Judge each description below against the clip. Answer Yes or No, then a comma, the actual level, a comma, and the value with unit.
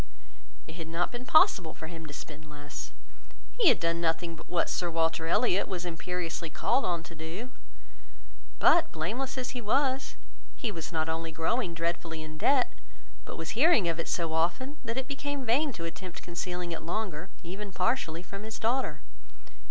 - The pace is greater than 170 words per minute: Yes, average, 180 wpm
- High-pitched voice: No, medium, 175 Hz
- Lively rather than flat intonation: Yes, wide, 6.5 semitones